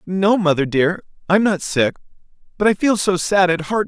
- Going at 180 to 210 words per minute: Yes, average, 200 wpm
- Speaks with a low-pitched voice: No, medium, 185 Hz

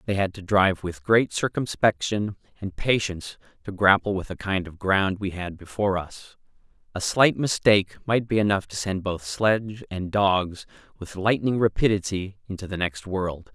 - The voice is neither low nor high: No, low, 100 Hz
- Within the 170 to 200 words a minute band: Yes, average, 175 wpm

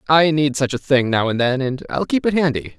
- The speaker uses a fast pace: Yes, fast, 280 wpm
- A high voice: No, medium, 140 Hz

